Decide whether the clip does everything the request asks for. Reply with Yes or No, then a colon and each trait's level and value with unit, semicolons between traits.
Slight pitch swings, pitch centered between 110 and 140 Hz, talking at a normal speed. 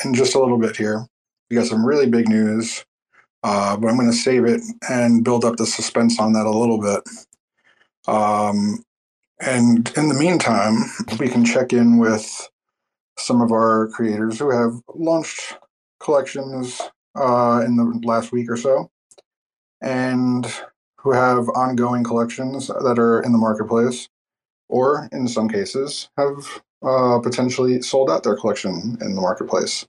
Yes: narrow, 2.2 semitones; low, 120 Hz; average, 155 wpm